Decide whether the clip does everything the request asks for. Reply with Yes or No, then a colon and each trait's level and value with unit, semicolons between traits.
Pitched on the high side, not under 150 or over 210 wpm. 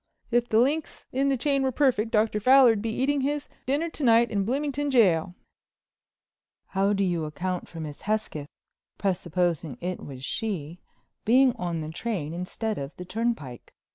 Yes: high, 215 Hz; average, 155 wpm